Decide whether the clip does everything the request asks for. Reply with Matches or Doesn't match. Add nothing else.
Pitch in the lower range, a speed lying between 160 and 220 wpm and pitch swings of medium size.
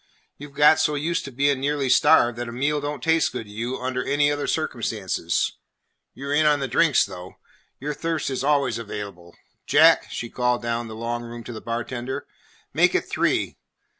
Matches